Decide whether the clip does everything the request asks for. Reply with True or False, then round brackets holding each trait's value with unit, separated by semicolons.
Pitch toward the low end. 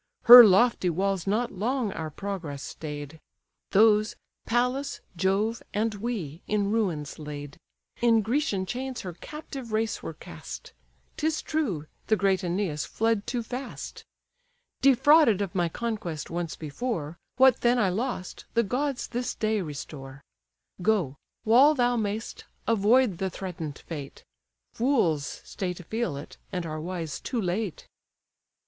False (205 Hz)